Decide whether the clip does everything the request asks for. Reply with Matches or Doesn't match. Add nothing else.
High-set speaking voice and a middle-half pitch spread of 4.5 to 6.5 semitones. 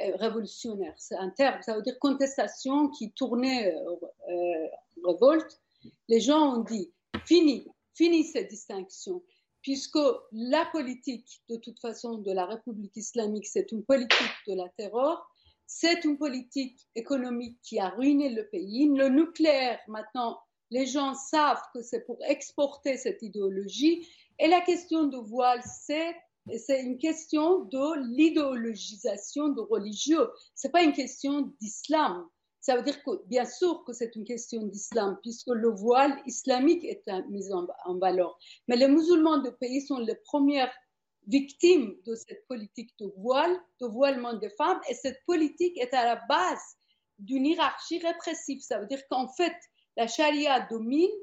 Matches